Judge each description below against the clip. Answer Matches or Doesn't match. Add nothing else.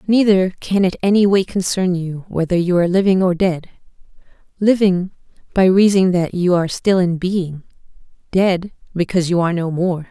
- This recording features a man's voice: Doesn't match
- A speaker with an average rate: Matches